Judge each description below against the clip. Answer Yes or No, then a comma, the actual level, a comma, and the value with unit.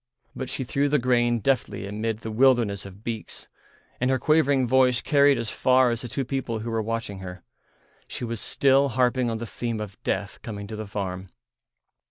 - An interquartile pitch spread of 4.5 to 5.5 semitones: No, average, 3.4 semitones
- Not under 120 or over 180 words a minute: No, average, 195 wpm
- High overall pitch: No, low, 115 Hz